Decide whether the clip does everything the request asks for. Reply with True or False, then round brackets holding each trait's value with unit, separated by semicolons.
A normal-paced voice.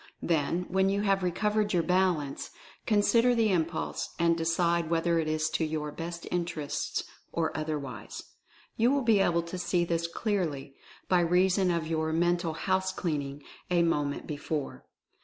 True (160 wpm)